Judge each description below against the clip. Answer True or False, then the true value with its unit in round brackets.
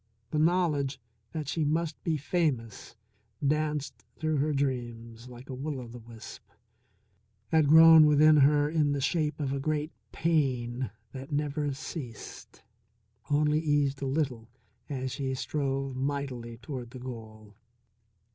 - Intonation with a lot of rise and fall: False (3.1 semitones)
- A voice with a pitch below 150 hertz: True (140 Hz)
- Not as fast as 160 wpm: True (135 wpm)